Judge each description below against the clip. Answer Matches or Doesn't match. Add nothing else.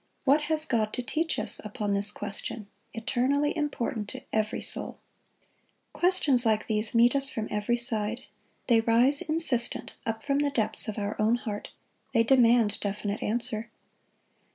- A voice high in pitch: Matches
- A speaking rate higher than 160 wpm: Doesn't match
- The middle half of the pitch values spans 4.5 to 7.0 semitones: Doesn't match